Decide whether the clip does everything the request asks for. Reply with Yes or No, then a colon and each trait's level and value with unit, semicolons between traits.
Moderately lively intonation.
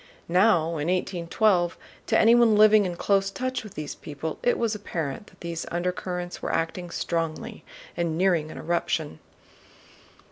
Yes: average, 4.0 semitones